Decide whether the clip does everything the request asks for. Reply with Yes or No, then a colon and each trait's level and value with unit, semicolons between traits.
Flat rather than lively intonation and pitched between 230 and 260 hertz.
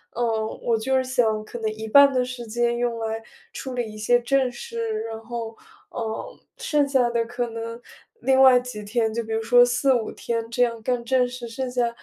Yes: narrow, 2.0 semitones; high, 240 Hz